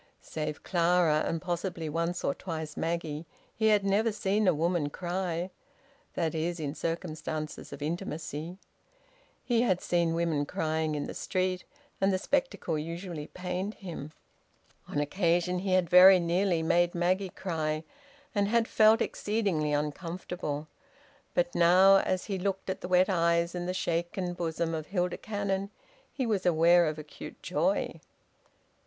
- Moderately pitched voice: Yes, medium, 175 Hz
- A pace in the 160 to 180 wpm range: No, average, 150 wpm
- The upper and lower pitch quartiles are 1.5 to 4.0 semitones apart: Yes, average, 2.8 semitones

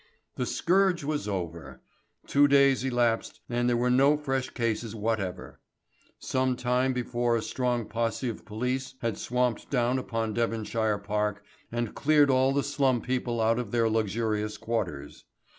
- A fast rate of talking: No, average, 150 wpm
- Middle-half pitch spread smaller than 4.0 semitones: Yes, average, 2.9 semitones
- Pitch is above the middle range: No, low, 120 Hz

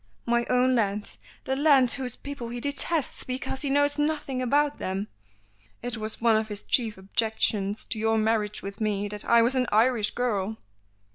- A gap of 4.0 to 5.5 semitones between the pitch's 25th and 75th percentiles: No, average, 3.6 semitones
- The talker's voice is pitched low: No, high, 235 Hz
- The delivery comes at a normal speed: Yes, average, 180 wpm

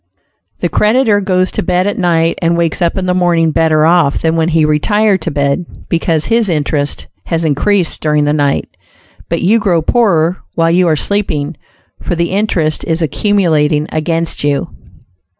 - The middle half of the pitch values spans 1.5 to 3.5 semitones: Yes, average, 3.0 semitones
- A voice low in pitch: No, medium, 165 Hz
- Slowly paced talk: No, average, 170 wpm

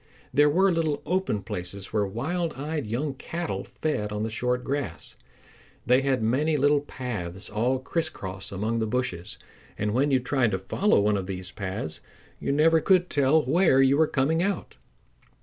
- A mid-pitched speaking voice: No, low, 130 Hz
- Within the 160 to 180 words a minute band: Yes, average, 175 wpm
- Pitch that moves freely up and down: Yes, wide, 6.4 semitones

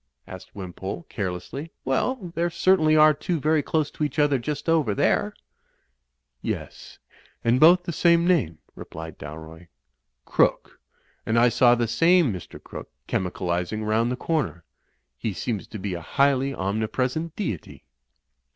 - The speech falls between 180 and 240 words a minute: No, average, 150 wpm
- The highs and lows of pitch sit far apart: Yes, wide, 8.7 semitones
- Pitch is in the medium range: No, low, 125 Hz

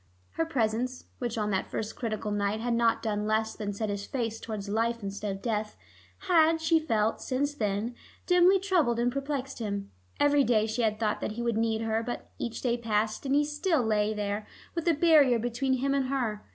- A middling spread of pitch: Yes, average, 4.3 semitones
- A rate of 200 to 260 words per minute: Yes, fast, 205 wpm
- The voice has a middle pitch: No, high, 230 Hz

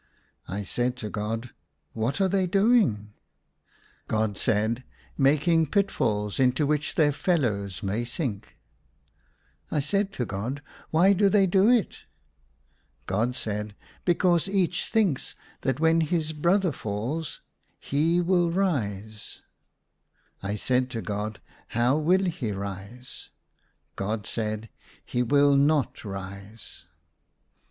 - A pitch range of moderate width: No, wide, 8.1 semitones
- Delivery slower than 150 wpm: Yes, slow, 135 wpm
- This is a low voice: Yes, low, 130 Hz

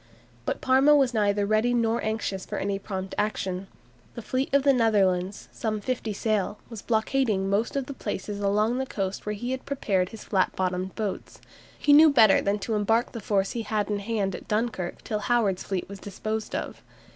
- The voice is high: Yes, high, 215 Hz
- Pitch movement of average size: Yes, average, 3.2 semitones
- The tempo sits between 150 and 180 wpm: No, average, 195 wpm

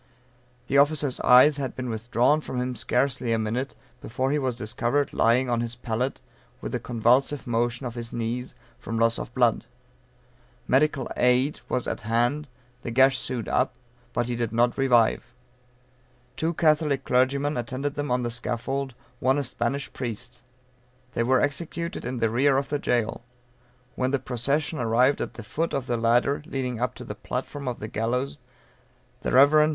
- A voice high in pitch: No, low, 125 Hz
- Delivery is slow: No, average, 175 wpm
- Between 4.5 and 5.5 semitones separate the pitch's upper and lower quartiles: No, average, 2.8 semitones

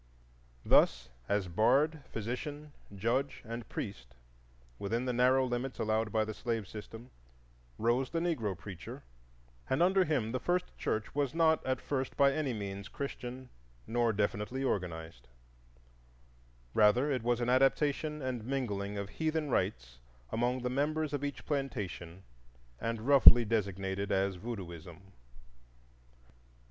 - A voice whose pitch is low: Yes, low, 120 Hz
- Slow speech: Yes, slow, 130 wpm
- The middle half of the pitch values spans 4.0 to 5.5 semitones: Yes, average, 5.2 semitones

